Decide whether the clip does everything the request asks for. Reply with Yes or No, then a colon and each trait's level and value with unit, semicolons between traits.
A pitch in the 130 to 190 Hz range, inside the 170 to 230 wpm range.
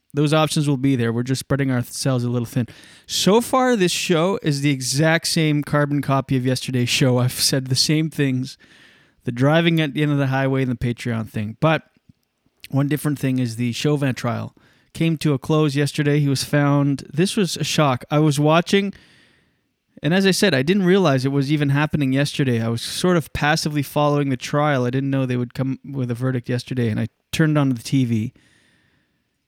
Yes: medium, 140 Hz; fast, 205 wpm